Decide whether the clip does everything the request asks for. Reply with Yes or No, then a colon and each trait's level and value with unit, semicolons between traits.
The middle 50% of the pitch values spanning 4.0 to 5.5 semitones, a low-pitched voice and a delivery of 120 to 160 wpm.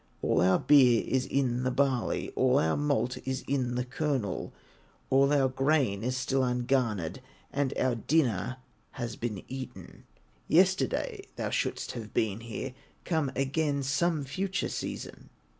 No: average, 2.8 semitones; low, 130 Hz; average, 140 wpm